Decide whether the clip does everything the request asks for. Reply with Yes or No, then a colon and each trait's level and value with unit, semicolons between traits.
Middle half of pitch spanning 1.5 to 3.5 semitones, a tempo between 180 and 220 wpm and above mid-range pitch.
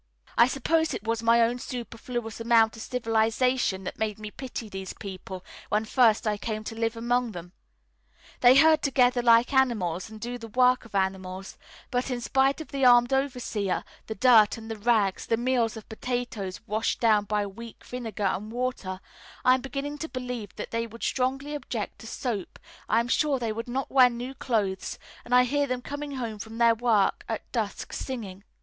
Yes: average, 2.8 semitones; average, 190 wpm; high, 235 Hz